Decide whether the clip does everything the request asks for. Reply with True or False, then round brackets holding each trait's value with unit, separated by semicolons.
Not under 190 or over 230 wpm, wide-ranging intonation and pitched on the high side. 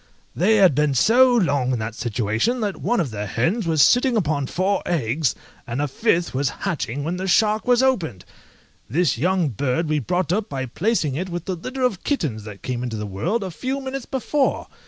False (205 wpm; 8.7 semitones; 165 Hz)